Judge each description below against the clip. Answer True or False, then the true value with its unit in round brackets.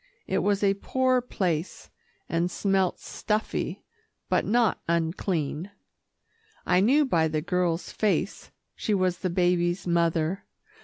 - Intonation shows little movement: False (3.2 semitones)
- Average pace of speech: False (120 wpm)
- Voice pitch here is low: False (180 Hz)